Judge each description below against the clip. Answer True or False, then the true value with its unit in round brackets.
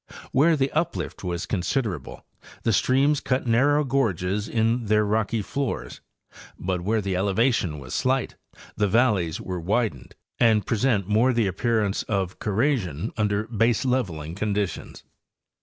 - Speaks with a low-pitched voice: True (110 Hz)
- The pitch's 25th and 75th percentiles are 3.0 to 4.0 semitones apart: False (4.6 semitones)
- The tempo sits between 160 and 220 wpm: False (135 wpm)